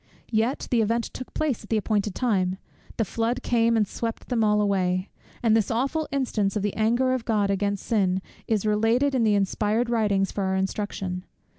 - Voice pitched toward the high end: Yes, high, 215 Hz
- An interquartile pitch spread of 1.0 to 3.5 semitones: Yes, average, 2.7 semitones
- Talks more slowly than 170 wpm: No, average, 190 wpm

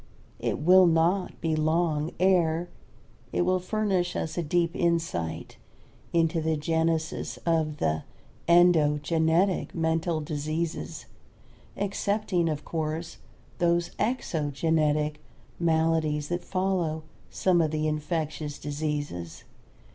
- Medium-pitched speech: Yes, medium, 160 Hz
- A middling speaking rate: No, slow, 100 wpm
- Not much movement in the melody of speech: Yes, narrow, 2.3 semitones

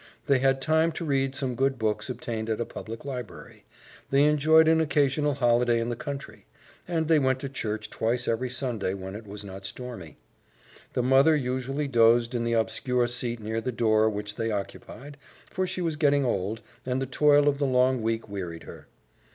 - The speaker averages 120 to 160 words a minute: No, average, 190 wpm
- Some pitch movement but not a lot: Yes, average, 3.8 semitones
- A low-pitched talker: Yes, low, 125 Hz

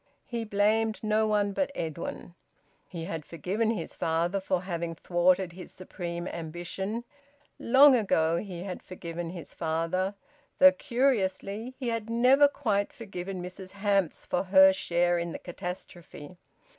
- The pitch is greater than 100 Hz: Yes, high, 190 Hz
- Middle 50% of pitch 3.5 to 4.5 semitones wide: Yes, average, 3.9 semitones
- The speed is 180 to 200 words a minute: No, average, 140 wpm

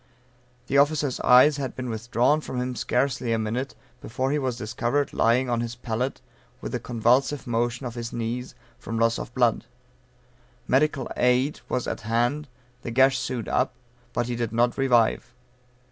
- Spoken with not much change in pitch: Yes, narrow, 2.1 semitones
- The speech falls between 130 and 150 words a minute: No, average, 165 wpm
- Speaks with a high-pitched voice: No, low, 125 Hz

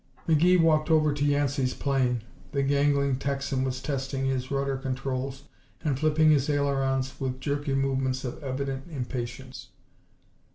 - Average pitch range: No, narrow, 1.6 semitones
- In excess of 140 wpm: No, slow, 135 wpm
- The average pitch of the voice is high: No, low, 135 Hz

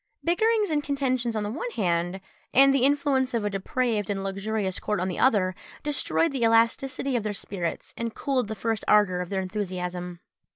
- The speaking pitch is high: Yes, high, 220 Hz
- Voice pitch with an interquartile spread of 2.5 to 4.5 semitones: No, wide, 5.6 semitones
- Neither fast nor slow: Yes, average, 190 wpm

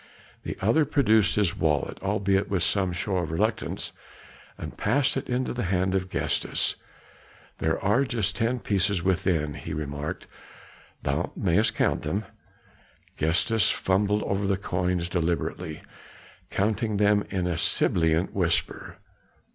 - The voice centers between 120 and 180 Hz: No, very low, 95 Hz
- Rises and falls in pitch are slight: No, average, 3.6 semitones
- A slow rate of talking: Yes, slow, 130 wpm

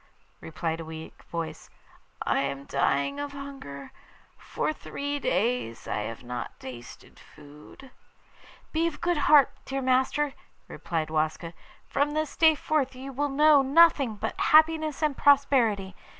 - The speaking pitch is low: No, very high, 265 Hz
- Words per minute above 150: No, slow, 135 wpm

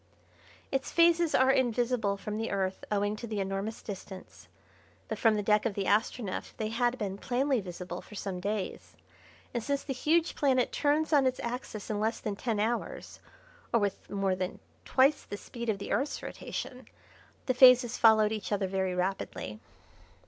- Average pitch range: Yes, average, 4.2 semitones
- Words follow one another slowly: No, average, 175 wpm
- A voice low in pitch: No, high, 220 Hz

